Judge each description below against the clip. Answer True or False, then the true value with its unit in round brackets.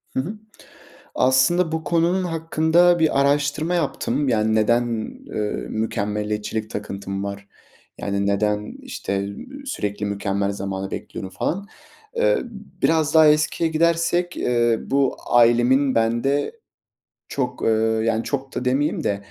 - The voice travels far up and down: True (7.3 semitones)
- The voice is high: False (130 Hz)